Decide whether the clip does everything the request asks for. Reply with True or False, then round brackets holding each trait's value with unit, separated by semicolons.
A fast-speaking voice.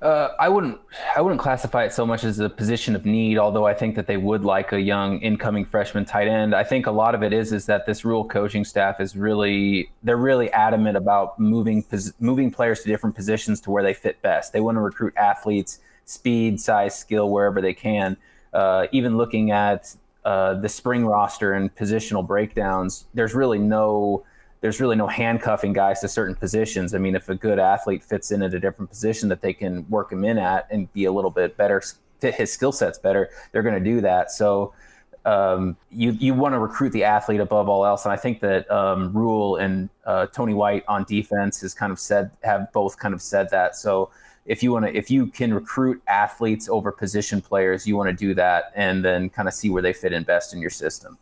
True (225 wpm)